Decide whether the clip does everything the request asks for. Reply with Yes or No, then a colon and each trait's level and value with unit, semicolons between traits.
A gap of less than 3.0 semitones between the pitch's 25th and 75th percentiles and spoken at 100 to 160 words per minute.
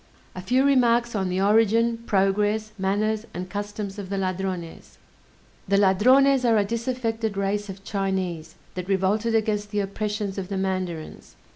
Yes: narrow, 2.6 semitones; average, 150 wpm